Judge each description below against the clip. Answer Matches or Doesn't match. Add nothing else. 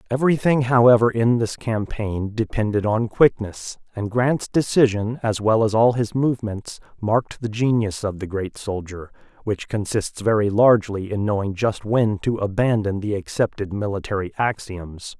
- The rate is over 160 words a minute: Doesn't match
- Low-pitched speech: Matches